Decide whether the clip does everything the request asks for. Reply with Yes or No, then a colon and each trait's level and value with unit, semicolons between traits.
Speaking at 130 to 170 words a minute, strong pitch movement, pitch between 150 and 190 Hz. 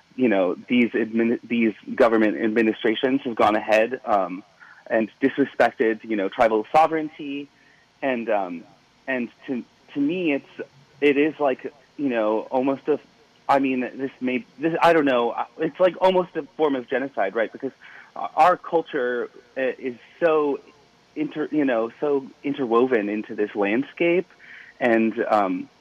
No: average, 145 wpm; wide, 5.7 semitones; low, 135 Hz